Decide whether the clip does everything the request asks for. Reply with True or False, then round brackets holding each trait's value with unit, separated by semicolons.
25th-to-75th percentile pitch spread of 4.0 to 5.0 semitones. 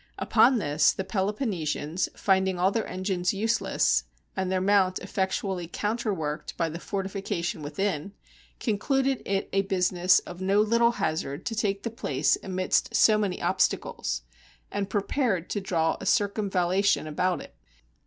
False (2.7 semitones)